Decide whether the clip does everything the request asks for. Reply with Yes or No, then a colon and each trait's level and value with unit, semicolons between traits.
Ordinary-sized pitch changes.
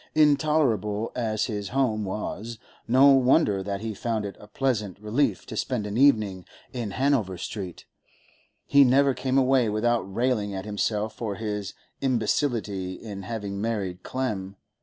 Yes: average, 4.1 semitones